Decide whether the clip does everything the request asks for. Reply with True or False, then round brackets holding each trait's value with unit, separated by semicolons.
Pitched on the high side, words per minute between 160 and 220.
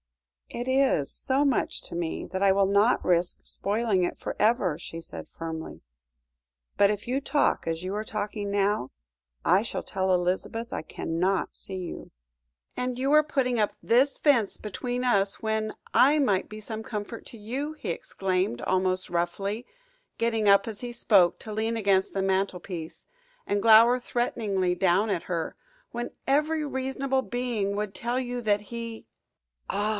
True (210 Hz; 165 wpm)